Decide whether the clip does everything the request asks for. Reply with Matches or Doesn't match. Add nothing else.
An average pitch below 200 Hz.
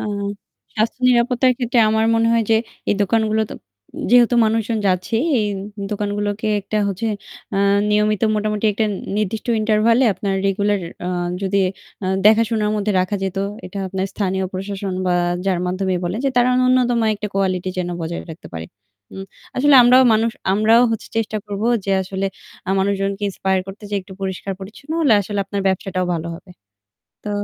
Doesn't match